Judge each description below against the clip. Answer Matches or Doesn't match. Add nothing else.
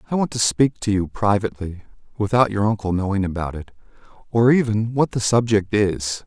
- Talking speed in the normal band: Matches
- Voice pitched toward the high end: Doesn't match